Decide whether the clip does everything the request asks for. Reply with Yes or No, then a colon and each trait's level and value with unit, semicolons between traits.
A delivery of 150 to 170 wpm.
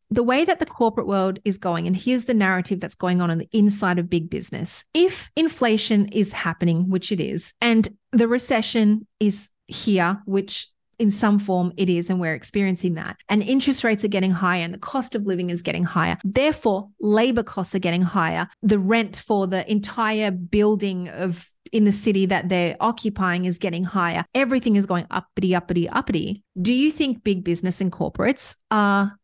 No: average, 190 wpm